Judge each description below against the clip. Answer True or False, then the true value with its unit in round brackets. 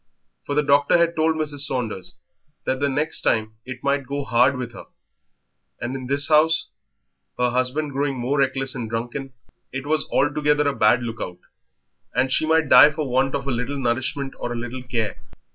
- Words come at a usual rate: True (190 wpm)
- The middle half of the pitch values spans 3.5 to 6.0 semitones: False (2.8 semitones)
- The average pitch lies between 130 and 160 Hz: True (135 Hz)